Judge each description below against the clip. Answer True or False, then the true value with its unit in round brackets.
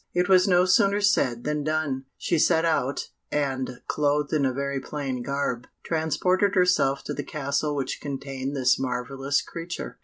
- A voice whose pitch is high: False (145 Hz)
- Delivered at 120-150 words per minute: False (160 wpm)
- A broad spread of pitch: False (3.7 semitones)